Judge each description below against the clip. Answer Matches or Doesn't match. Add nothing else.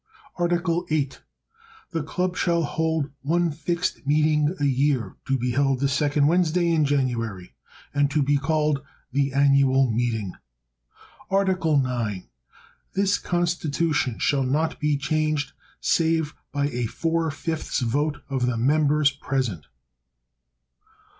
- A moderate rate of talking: Doesn't match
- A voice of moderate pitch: Matches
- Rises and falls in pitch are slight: Doesn't match